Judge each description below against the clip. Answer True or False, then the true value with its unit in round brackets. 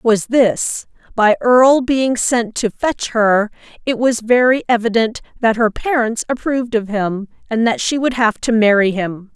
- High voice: True (230 Hz)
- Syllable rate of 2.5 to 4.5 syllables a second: True (4.4 syllables/s)